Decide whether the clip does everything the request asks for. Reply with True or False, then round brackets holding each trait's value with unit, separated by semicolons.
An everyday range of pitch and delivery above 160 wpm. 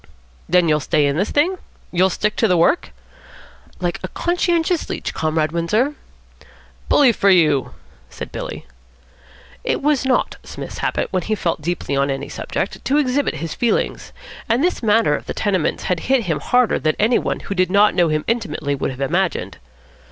False (7.6 semitones; 180 wpm)